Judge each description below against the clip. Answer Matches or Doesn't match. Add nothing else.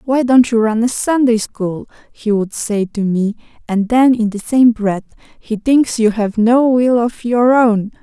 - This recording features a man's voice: Doesn't match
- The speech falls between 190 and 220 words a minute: Matches